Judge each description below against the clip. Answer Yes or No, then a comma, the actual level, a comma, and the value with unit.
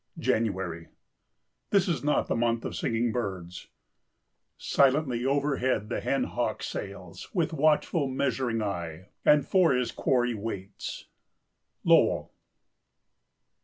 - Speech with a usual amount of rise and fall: No, wide, 5.9 semitones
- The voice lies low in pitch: Yes, low, 120 Hz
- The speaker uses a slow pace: Yes, slow, 110 wpm